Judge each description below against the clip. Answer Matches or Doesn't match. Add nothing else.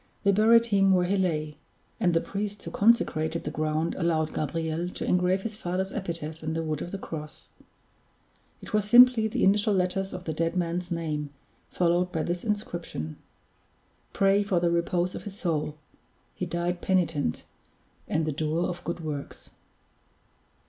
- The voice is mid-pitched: Matches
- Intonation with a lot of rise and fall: Doesn't match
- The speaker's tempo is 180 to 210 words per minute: Doesn't match